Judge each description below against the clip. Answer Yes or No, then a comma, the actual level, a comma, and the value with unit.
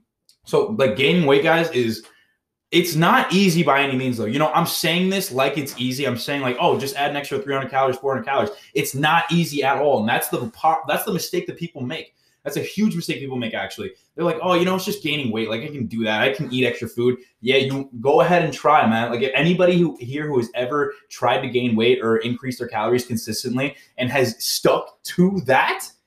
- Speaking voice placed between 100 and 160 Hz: Yes, medium, 140 Hz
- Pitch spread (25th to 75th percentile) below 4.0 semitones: No, average, 5.2 semitones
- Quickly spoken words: Yes, fast, 235 wpm